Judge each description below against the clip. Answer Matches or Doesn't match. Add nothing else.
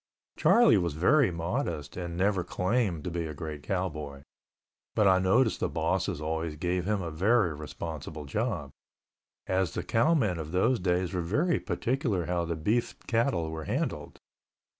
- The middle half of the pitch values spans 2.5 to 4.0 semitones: Doesn't match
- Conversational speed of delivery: Matches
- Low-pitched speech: Matches